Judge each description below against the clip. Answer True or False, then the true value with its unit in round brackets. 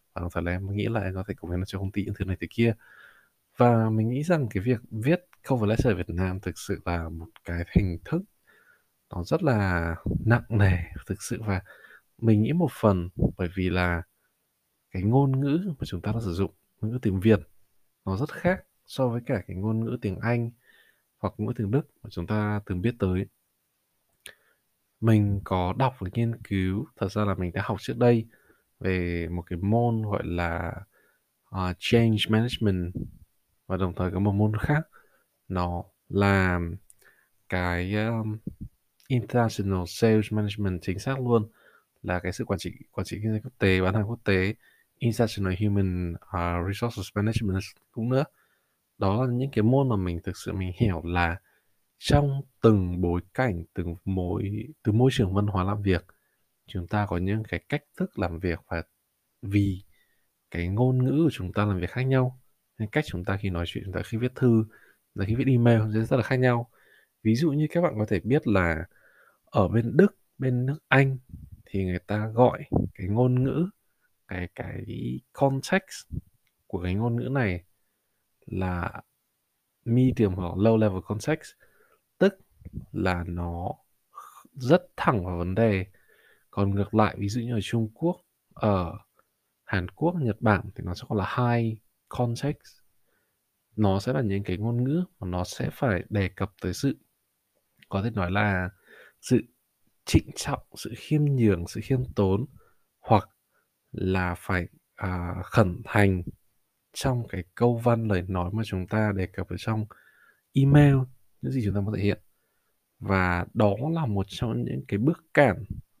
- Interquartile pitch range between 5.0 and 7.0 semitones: False (4.5 semitones)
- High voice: False (105 Hz)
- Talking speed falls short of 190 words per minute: True (180 wpm)